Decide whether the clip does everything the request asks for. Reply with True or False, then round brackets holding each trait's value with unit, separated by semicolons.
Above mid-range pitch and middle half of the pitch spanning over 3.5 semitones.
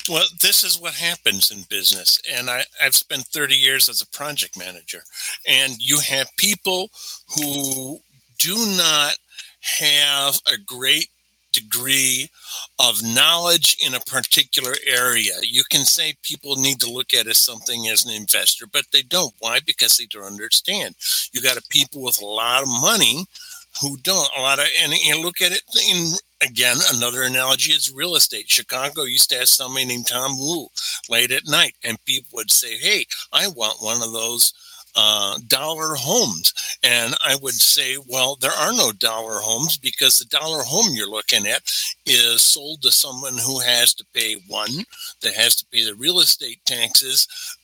False (140 Hz; 4.7 semitones)